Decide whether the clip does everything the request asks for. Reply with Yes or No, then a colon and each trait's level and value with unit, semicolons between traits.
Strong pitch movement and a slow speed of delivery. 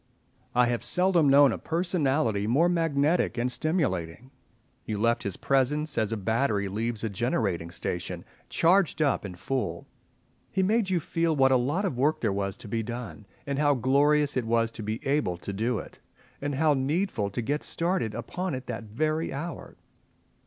No: wide, 5.9 semitones; average, 180 wpm